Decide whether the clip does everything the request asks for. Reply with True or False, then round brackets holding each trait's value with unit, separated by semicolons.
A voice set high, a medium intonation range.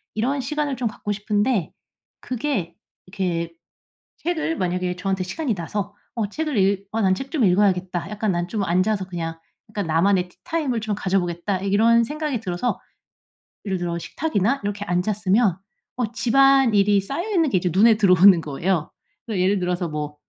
True (200 Hz; 4.3 semitones)